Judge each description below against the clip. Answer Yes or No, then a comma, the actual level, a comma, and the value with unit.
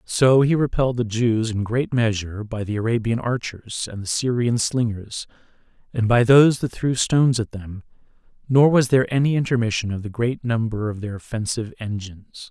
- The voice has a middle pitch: No, low, 115 Hz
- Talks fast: No, average, 180 wpm